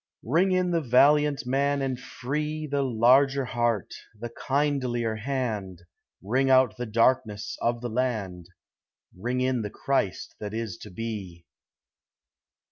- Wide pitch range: No, average, 4.0 semitones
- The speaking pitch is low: Yes, low, 125 Hz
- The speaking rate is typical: No, slow, 130 wpm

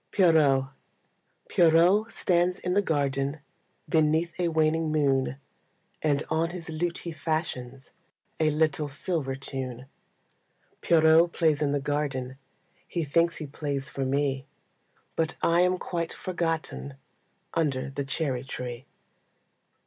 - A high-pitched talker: No, medium, 155 Hz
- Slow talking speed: Yes, slow, 120 wpm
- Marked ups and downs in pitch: No, average, 3.3 semitones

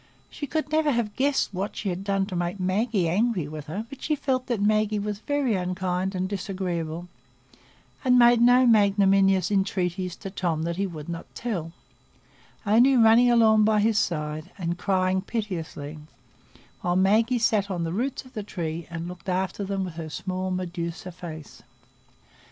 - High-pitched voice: Yes, high, 195 Hz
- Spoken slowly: No, average, 170 wpm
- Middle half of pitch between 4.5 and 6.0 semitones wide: No, average, 4.0 semitones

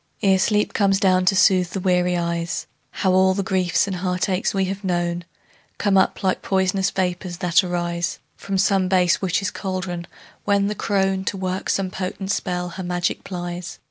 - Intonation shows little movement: Yes, narrow, 1.5 semitones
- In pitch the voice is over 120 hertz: Yes, medium, 185 Hz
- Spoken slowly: No, average, 175 wpm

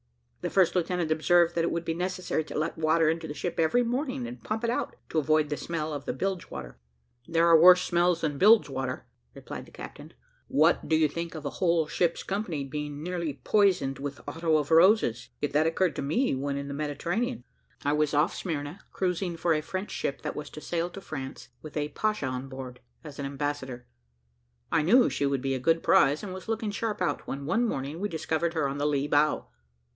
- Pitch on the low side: No, medium, 160 Hz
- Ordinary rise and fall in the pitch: Yes, average, 3.8 semitones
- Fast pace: Yes, fast, 220 wpm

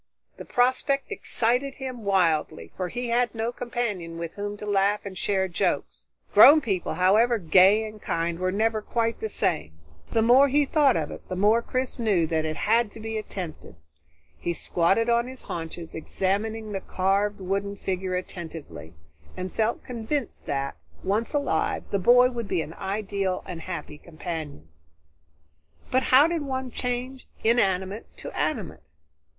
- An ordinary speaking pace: Yes, average, 155 wpm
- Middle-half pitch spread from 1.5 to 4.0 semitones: No, average, 4.7 semitones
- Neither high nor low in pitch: No, high, 205 Hz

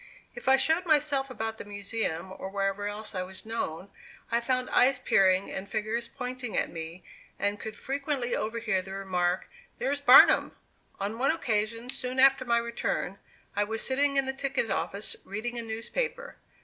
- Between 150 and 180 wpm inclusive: Yes, average, 170 wpm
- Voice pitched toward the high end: Yes, high, 230 Hz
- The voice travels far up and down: No, average, 4.9 semitones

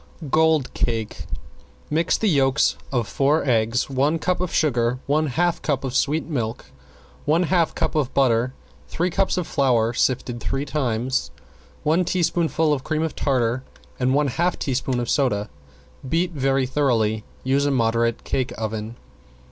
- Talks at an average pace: Yes, average, 155 wpm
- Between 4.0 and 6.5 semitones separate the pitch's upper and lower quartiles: Yes, average, 4.5 semitones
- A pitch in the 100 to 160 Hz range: Yes, low, 135 Hz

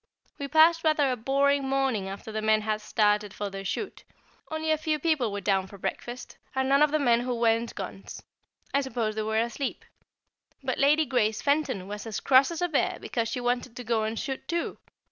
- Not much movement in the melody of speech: No, average, 4.6 semitones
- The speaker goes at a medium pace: No, fast, 210 wpm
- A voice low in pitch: No, high, 245 Hz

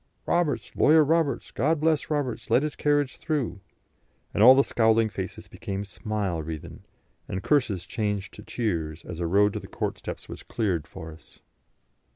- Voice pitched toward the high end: No, low, 110 Hz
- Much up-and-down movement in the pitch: Yes, wide, 7.3 semitones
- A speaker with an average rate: Yes, average, 170 wpm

